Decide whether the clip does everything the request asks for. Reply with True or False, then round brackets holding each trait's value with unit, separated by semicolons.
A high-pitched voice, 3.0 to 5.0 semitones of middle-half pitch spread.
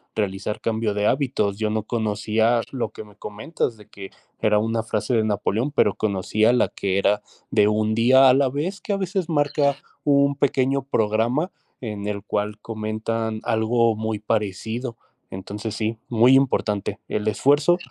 False (110 Hz; 3.6 semitones)